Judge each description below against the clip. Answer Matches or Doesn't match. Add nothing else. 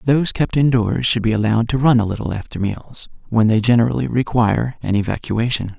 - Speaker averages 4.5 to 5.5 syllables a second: Doesn't match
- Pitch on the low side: Matches